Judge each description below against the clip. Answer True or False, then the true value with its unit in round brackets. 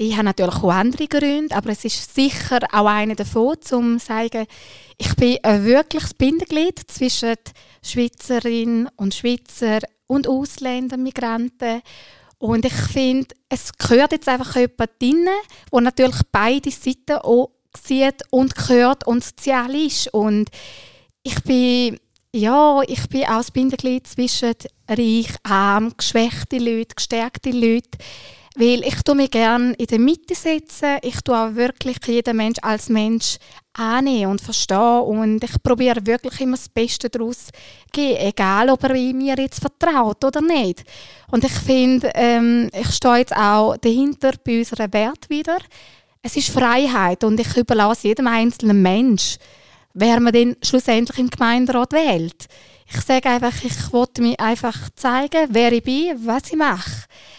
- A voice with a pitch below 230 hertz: False (245 Hz)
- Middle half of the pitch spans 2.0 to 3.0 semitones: True (2.5 semitones)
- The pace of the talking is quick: False (150 wpm)